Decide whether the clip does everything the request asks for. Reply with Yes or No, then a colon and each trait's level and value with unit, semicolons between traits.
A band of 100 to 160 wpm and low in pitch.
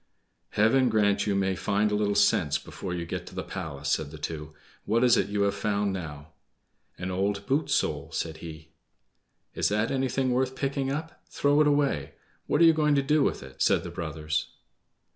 No: average, 200 wpm; low, 100 Hz